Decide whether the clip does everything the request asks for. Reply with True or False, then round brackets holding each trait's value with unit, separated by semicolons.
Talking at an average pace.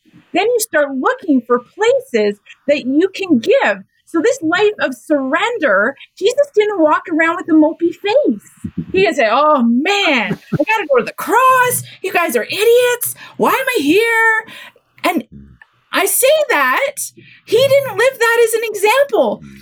True (160 wpm)